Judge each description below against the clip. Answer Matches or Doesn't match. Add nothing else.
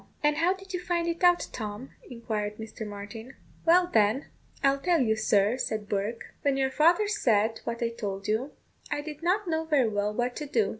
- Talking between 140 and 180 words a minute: Doesn't match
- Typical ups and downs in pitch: Doesn't match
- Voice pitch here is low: Doesn't match